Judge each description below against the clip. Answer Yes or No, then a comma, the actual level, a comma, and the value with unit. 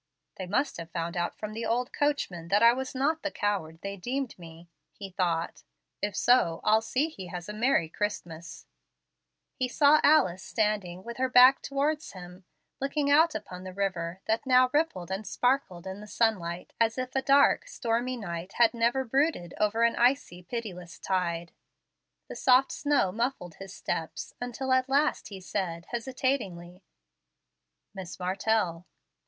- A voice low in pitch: No, high, 215 Hz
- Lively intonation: Yes, wide, 6.2 semitones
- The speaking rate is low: No, average, 160 wpm